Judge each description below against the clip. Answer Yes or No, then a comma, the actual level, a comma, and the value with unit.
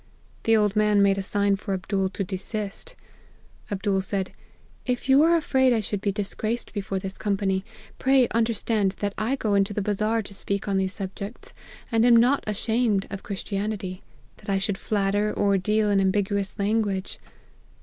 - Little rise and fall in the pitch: Yes, narrow, 2.1 semitones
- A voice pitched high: Yes, high, 205 Hz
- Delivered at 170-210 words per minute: Yes, average, 175 wpm